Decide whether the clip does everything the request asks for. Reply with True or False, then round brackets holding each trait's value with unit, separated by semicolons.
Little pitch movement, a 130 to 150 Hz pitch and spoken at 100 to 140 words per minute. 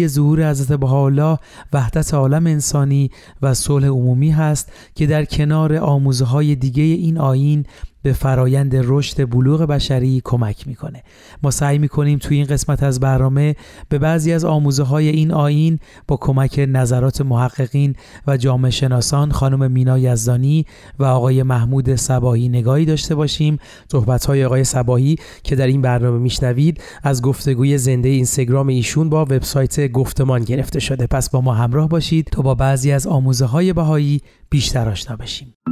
False (2.3 semitones; 135 Hz; 155 wpm)